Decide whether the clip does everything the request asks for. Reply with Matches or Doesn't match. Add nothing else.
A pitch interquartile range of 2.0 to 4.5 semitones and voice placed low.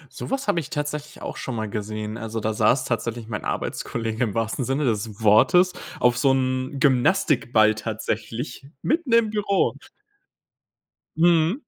Doesn't match